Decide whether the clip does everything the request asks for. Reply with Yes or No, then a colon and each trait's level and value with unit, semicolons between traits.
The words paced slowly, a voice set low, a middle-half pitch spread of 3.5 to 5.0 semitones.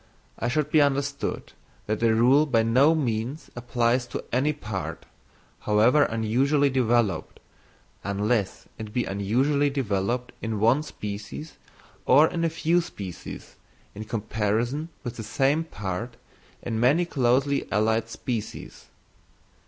Yes: slow, 125 wpm; low, 120 Hz; average, 4.6 semitones